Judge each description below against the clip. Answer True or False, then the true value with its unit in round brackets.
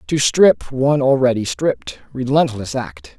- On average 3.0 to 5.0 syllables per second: True (4.5 syllables/s)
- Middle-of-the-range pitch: False (125 Hz)